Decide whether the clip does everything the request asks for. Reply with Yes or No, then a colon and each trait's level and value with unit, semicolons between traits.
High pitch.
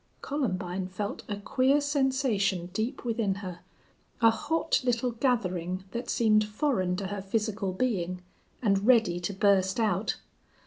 Yes: high, 210 Hz